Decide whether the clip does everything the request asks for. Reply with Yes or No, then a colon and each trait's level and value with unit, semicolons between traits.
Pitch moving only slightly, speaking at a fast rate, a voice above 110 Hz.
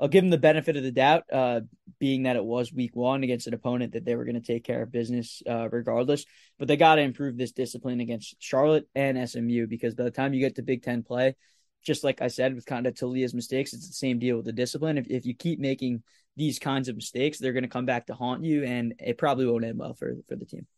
Yes: narrow, 2.3 semitones; fast, 270 wpm; low, 130 Hz